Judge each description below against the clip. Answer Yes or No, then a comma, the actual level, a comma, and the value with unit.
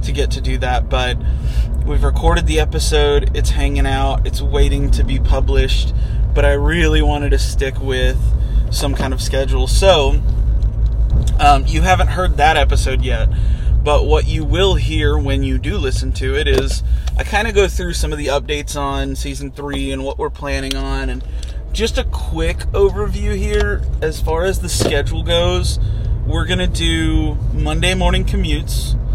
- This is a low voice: Yes, very low, 80 Hz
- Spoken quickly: No, average, 175 wpm